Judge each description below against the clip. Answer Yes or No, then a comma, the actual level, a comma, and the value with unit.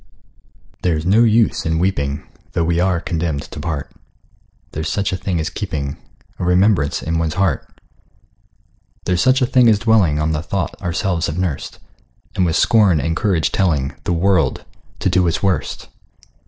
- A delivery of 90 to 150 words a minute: No, average, 170 wpm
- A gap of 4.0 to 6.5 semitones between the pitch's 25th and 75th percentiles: No, average, 3.5 semitones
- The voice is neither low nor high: No, very low, 85 Hz